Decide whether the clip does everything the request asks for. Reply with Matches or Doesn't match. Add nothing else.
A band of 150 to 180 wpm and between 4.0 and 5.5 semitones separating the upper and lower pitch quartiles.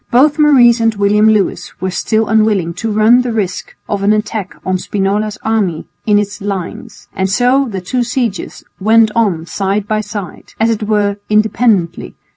Doesn't match